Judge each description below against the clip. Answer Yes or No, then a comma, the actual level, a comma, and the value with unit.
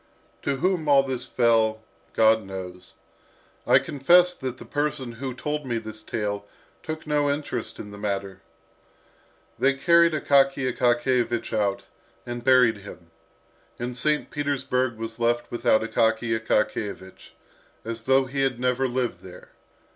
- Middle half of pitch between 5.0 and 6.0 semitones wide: No, average, 3.6 semitones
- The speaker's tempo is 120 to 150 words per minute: Yes, average, 140 wpm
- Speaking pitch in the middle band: No, low, 120 Hz